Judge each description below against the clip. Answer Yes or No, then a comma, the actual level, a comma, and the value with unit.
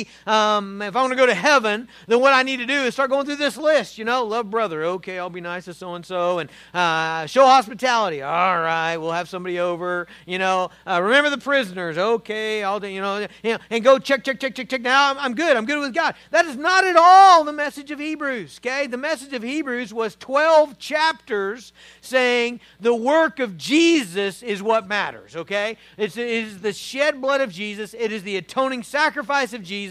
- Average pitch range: No, wide, 5.9 semitones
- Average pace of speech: No, fast, 215 wpm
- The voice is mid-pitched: No, high, 235 Hz